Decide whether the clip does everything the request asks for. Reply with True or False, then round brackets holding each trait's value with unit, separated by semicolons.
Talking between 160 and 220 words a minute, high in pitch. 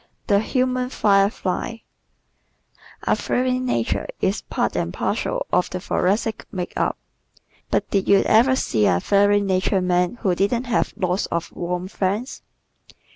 False (140 wpm; 200 Hz)